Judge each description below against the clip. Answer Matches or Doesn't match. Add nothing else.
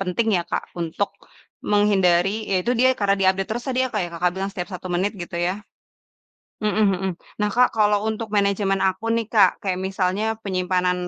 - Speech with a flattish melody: Matches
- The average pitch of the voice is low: Doesn't match